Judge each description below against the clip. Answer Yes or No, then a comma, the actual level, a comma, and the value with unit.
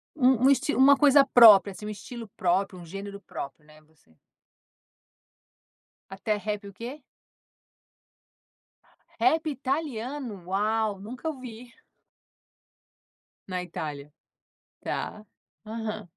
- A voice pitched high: Yes, high, 215 Hz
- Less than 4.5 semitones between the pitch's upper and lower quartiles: No, average, 4.9 semitones